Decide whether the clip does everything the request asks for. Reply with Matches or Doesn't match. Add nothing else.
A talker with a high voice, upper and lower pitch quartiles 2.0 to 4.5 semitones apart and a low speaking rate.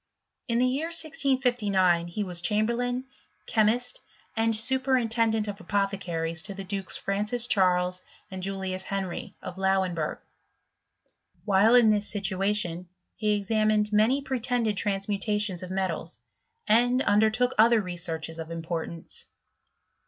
Matches